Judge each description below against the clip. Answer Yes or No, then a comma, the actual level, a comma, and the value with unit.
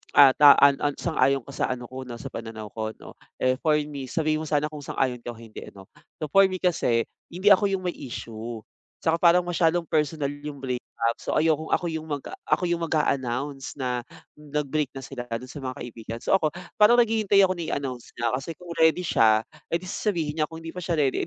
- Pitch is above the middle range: No, medium, 145 Hz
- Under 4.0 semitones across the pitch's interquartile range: No, average, 4.6 semitones